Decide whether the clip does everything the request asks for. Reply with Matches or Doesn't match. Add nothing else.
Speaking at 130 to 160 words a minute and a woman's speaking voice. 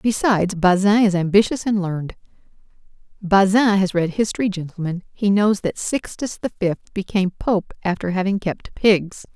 Matches